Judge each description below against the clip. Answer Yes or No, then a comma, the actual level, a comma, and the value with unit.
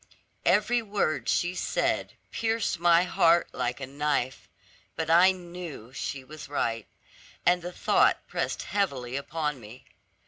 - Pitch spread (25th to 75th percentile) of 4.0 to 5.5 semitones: Yes, average, 4.8 semitones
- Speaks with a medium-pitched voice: Yes, medium, 160 Hz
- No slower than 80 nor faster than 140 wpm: Yes, slow, 135 wpm